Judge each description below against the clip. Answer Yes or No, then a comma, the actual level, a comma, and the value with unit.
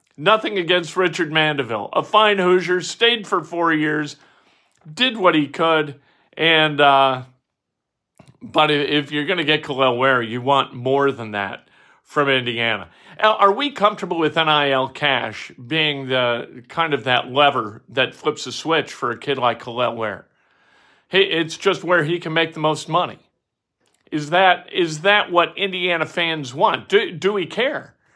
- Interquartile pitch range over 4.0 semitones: Yes, average, 4.7 semitones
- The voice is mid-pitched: Yes, medium, 155 Hz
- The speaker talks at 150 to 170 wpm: Yes, average, 160 wpm